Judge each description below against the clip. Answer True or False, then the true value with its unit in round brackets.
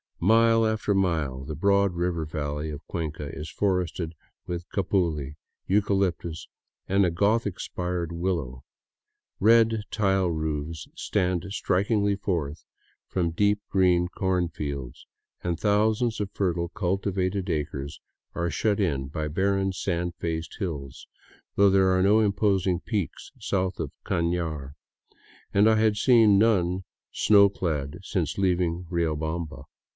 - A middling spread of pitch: True (3.6 semitones)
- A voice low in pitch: True (90 Hz)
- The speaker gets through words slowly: True (125 wpm)